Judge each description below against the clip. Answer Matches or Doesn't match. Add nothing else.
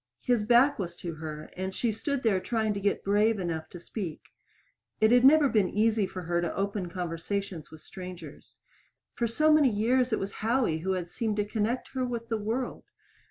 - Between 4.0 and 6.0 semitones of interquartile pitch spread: Matches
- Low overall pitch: Doesn't match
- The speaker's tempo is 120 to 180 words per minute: Doesn't match